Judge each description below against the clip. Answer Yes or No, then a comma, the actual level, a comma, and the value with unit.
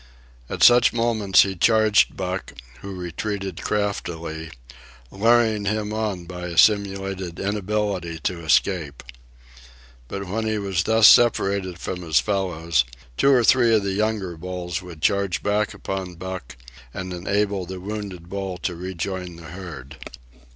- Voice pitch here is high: No, very low, 95 Hz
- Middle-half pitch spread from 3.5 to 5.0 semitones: No, average, 2.9 semitones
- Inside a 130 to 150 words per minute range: Yes, average, 140 wpm